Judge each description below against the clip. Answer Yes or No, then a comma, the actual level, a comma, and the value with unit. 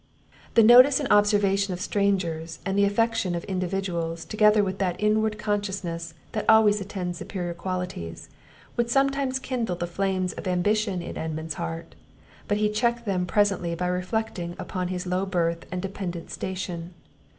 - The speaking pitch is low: No, high, 190 Hz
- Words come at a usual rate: Yes, average, 155 wpm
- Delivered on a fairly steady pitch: No, average, 3.2 semitones